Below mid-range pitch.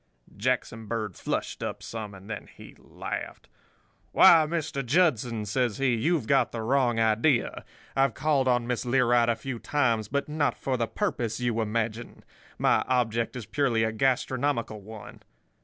Yes: low, 120 Hz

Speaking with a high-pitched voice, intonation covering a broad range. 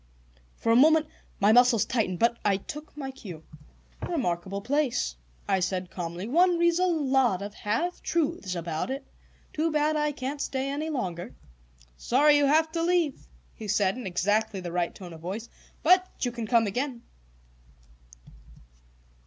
Yes: high, 245 Hz; wide, 7.5 semitones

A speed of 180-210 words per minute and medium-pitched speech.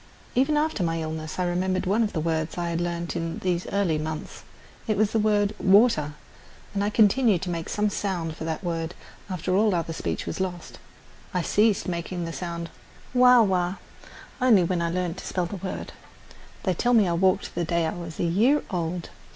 Yes: average, 200 wpm; medium, 180 Hz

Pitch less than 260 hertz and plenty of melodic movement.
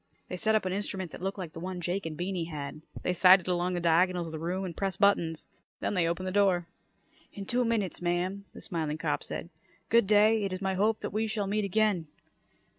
No: medium, 185 Hz; narrow, 2.6 semitones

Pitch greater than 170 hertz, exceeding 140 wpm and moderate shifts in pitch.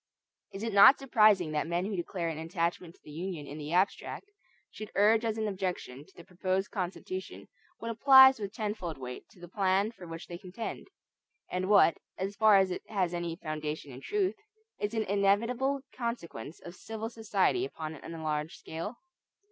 Yes: high, 190 Hz; average, 180 wpm; average, 4.5 semitones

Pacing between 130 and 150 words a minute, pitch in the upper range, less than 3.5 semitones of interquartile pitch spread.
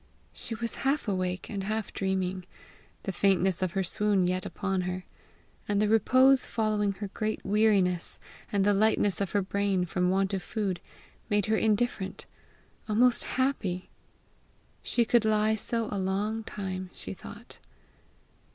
Yes: average, 145 wpm; high, 200 Hz; narrow, 2.5 semitones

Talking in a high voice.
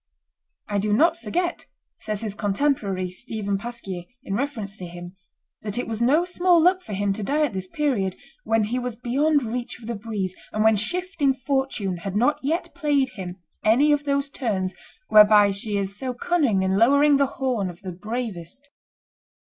Yes: high, 225 Hz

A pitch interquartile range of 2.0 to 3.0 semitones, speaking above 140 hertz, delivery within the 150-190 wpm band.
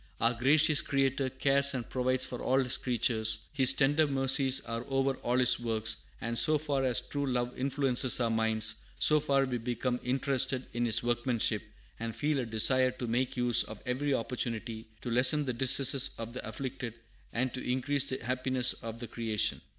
No: narrow, 2.4 semitones; low, 125 Hz; average, 180 wpm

